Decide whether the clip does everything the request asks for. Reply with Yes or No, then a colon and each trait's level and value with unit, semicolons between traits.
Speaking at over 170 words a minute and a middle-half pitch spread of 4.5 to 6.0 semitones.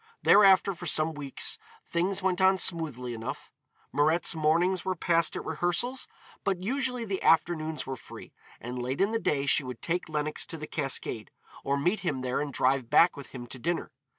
Yes: average, 185 wpm; average, 5.1 semitones